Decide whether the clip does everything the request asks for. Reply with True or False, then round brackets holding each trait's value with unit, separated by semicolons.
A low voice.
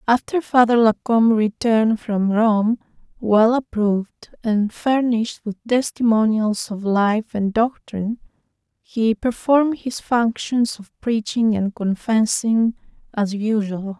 False (225 Hz)